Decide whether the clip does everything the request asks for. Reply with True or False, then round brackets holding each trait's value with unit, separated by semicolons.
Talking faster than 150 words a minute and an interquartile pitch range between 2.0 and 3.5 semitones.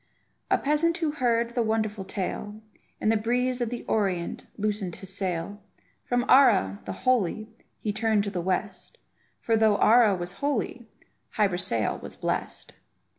False (160 wpm; 3.9 semitones)